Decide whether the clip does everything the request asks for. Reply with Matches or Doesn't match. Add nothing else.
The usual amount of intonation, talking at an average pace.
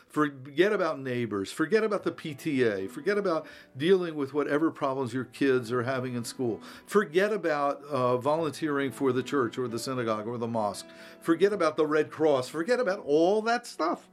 Matches